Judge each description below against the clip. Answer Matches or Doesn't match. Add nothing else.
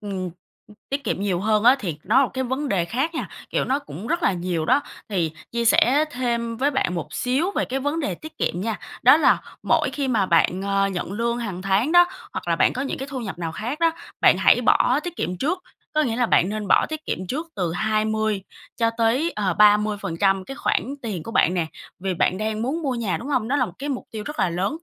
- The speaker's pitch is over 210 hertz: Matches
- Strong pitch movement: Matches